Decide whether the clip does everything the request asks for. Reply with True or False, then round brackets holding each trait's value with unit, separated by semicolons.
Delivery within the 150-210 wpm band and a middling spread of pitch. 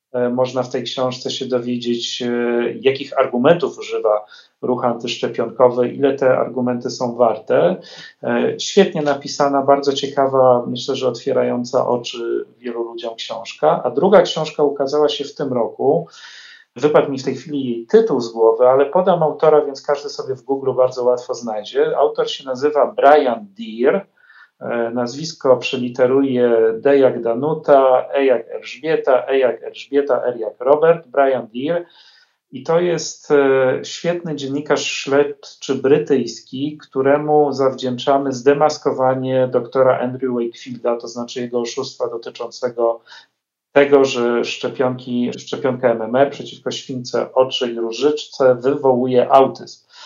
False (125 wpm; 3.2 semitones)